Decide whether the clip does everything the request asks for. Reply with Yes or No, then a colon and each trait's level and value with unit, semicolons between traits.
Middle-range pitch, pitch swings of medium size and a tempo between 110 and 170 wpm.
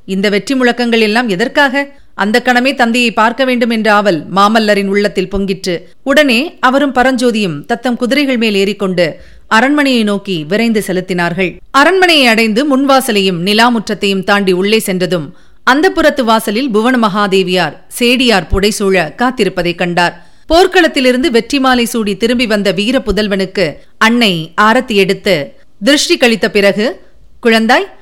No: high, 220 Hz; average, 4.3 semitones; average, 120 wpm